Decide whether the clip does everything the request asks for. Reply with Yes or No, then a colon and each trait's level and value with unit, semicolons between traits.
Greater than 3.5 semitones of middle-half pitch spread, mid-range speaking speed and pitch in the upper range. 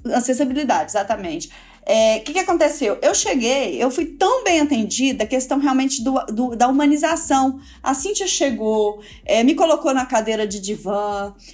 Yes: average, 5.2 semitones; average, 160 wpm; very high, 265 Hz